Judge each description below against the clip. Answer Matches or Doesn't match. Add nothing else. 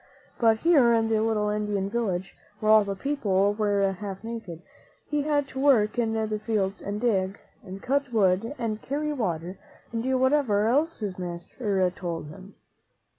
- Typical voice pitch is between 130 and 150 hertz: Doesn't match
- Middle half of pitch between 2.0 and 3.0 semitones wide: Doesn't match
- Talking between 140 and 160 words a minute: Doesn't match